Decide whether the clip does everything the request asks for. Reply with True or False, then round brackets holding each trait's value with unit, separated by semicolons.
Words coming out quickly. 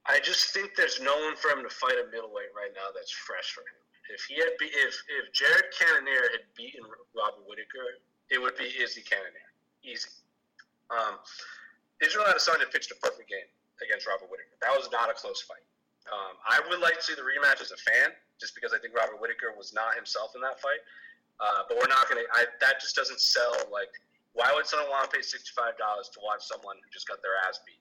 True (220 wpm)